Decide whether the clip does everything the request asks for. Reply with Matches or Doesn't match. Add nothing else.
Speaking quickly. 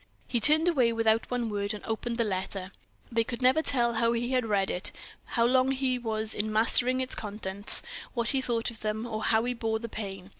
Matches